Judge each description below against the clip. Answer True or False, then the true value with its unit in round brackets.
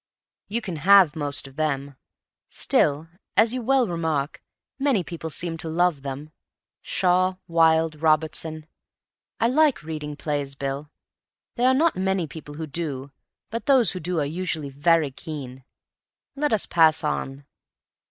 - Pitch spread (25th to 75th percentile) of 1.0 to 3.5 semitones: False (4.1 semitones)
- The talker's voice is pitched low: False (160 Hz)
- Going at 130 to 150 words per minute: True (145 wpm)